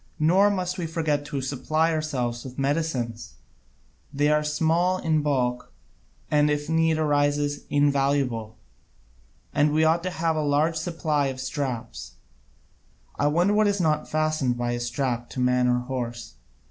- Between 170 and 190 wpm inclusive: No, average, 150 wpm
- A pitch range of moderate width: Yes, average, 3.9 semitones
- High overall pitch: No, medium, 145 Hz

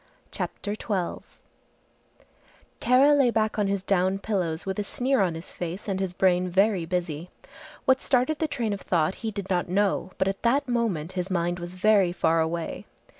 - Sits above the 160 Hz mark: Yes, high, 190 Hz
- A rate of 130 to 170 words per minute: No, average, 180 wpm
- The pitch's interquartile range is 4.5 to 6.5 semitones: No, average, 3.6 semitones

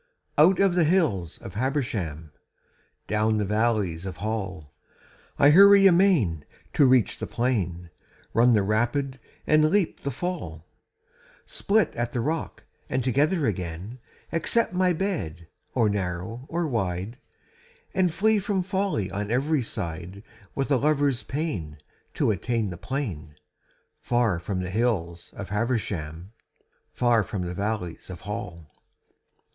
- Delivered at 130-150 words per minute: Yes, slow, 135 wpm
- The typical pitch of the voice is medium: No, low, 115 Hz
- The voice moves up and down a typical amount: No, wide, 8.5 semitones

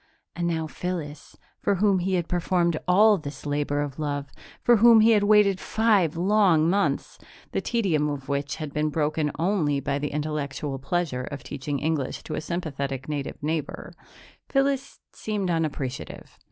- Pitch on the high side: No, medium, 160 Hz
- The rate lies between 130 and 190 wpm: Yes, average, 160 wpm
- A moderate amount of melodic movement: Yes, average, 4.7 semitones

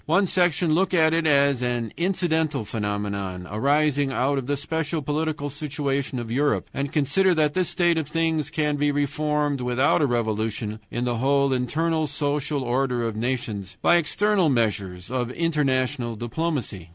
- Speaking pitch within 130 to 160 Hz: Yes, medium, 140 Hz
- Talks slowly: No, average, 160 wpm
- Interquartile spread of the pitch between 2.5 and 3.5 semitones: No, average, 4.5 semitones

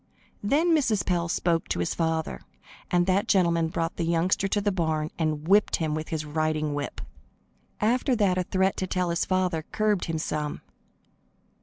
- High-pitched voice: No, medium, 170 Hz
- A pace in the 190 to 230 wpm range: No, average, 175 wpm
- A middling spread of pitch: Yes, average, 3.5 semitones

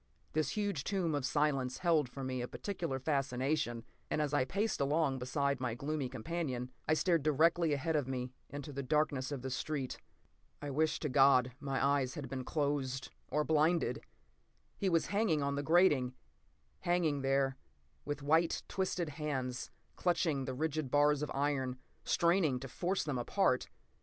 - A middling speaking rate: Yes, average, 165 wpm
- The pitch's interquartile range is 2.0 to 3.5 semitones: Yes, average, 3.1 semitones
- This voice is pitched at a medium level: Yes, medium, 145 Hz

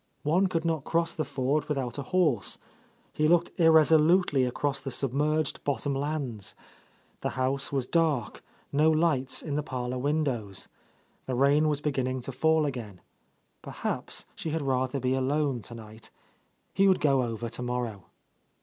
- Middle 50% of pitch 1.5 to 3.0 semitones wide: No, average, 3.5 semitones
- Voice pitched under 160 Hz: Yes, medium, 140 Hz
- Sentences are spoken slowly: No, average, 155 wpm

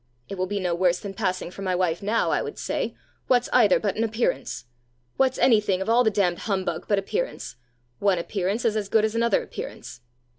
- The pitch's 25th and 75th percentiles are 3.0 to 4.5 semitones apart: Yes, average, 3.4 semitones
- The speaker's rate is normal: No, fast, 215 wpm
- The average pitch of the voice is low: No, high, 200 Hz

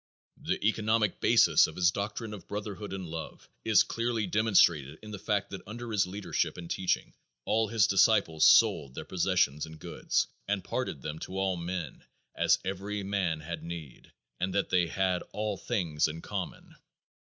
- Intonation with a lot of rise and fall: No, average, 3.7 semitones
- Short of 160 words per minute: No, average, 170 wpm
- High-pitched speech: No, very low, 95 Hz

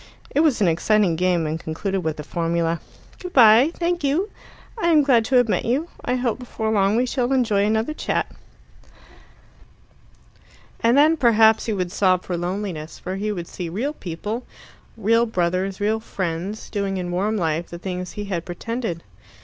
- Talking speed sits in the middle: Yes, average, 175 wpm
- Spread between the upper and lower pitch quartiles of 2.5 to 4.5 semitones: No, average, 5.3 semitones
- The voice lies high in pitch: Yes, high, 205 Hz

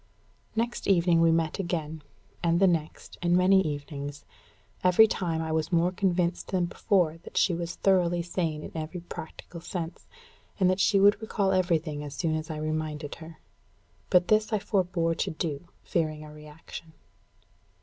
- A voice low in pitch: No, medium, 170 Hz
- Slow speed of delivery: No, average, 165 wpm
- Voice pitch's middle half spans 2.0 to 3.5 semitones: Yes, narrow, 2.6 semitones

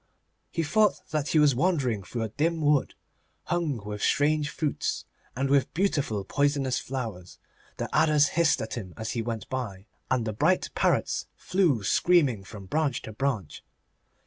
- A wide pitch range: Yes, wide, 5.7 semitones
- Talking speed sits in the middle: Yes, average, 160 wpm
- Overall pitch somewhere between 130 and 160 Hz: Yes, low, 135 Hz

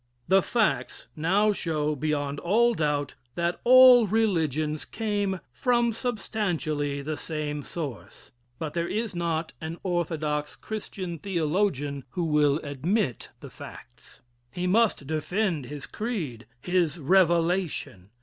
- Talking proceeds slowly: Yes, slow, 120 wpm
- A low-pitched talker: No, medium, 170 Hz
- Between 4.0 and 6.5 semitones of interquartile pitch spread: Yes, average, 5.3 semitones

